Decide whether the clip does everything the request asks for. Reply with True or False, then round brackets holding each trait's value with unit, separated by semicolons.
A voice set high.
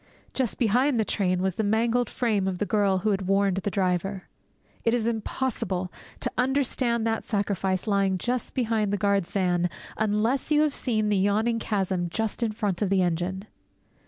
True (205 Hz)